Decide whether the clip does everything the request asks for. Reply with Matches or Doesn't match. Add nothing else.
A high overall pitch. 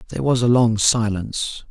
Doesn't match